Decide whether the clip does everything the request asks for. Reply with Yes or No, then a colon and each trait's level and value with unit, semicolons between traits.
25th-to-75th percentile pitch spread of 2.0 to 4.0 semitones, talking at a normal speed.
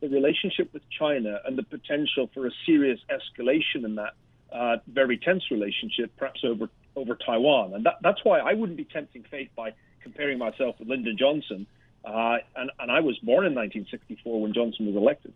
No: average, 4.5 semitones; average, 190 wpm